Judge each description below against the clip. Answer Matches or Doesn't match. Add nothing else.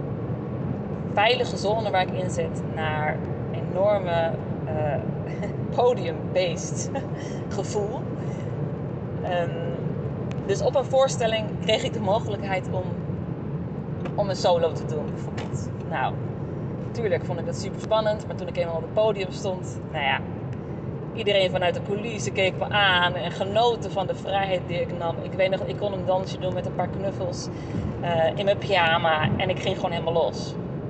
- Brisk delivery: Doesn't match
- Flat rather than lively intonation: Doesn't match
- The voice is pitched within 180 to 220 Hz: Doesn't match